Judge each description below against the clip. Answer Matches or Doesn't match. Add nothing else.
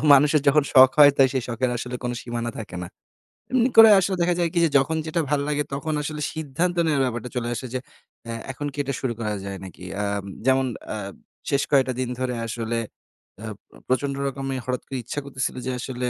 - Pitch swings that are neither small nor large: Matches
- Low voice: Matches